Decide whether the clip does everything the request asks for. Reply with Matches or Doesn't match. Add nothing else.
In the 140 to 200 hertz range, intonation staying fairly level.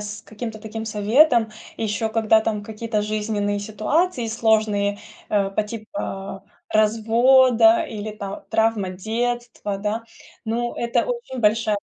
Doesn't match